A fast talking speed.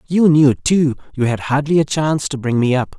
Yes: fast, 240 wpm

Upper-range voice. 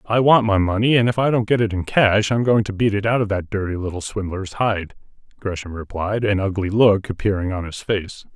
No: low, 105 Hz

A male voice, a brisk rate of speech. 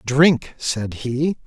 No: male; slow, 125 wpm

